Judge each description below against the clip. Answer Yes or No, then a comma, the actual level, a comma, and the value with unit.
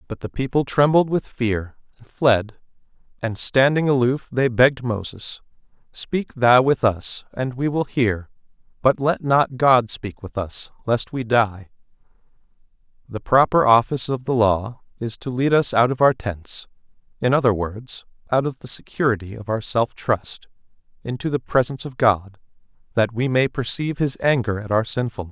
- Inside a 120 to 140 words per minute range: No, average, 165 wpm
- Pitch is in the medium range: No, low, 120 Hz